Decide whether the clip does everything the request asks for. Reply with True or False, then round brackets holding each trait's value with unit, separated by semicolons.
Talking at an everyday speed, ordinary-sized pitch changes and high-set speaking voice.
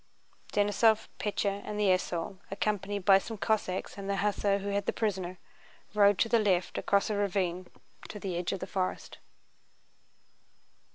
False (160 wpm; 1.8 semitones; 200 Hz)